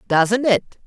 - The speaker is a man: No, female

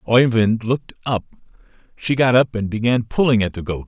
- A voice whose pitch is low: Yes, low, 115 Hz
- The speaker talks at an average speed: Yes, average, 185 wpm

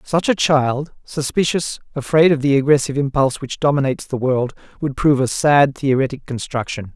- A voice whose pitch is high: No, medium, 140 Hz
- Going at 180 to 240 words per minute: No, average, 165 wpm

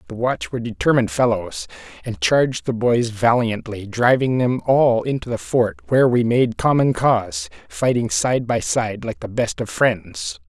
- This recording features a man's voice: Yes, male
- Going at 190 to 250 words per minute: No, average, 170 wpm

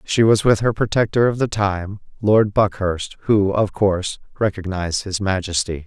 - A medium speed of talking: Yes, average, 165 wpm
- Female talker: No, male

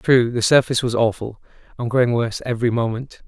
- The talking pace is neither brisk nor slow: Yes, average, 185 wpm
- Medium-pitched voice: No, low, 120 Hz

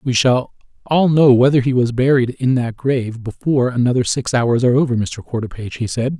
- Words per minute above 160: Yes, fast, 205 wpm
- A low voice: Yes, low, 125 Hz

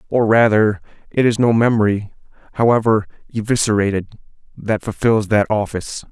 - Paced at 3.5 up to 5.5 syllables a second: Yes, 5.4 syllables/s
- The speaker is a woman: No, male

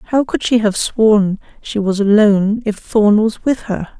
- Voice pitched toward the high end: Yes, high, 215 Hz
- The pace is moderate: Yes, average, 195 wpm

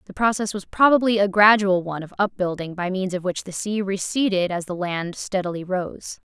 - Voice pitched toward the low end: No, high, 190 Hz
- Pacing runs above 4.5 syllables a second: Yes, 5.3 syllables/s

